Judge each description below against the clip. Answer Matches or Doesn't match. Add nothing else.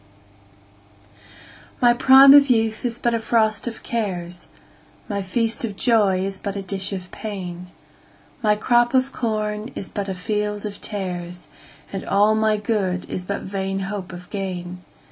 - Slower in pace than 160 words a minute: Matches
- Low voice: Doesn't match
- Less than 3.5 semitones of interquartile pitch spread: Matches